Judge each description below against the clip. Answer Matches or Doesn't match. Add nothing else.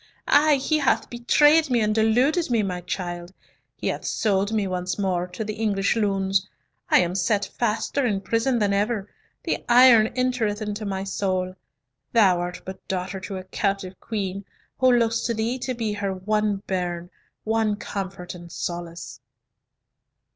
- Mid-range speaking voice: Doesn't match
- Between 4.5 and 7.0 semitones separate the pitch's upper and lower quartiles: Doesn't match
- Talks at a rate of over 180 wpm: Doesn't match